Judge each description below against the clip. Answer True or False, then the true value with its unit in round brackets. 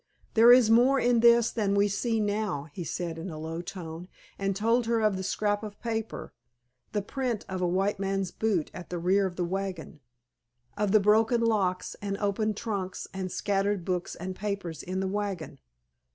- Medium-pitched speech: False (200 Hz)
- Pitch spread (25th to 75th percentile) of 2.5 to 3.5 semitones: True (3.0 semitones)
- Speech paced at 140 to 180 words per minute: False (190 wpm)